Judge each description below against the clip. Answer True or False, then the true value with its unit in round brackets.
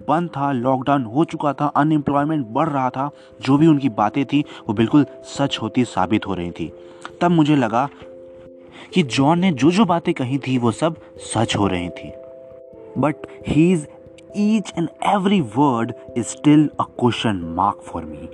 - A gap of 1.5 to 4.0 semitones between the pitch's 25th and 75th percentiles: False (5.4 semitones)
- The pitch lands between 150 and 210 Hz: False (140 Hz)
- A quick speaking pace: False (175 wpm)